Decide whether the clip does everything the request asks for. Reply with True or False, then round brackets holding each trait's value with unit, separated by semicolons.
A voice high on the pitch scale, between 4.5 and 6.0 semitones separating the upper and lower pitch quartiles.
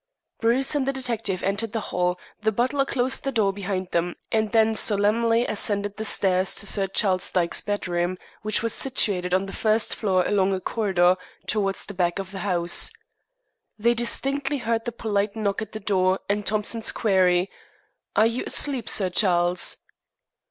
False (205 Hz; 3.3 semitones)